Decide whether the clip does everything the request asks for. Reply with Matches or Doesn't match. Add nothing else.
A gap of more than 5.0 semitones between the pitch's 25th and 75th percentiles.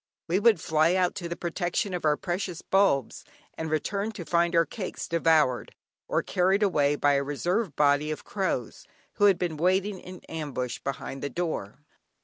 Doesn't match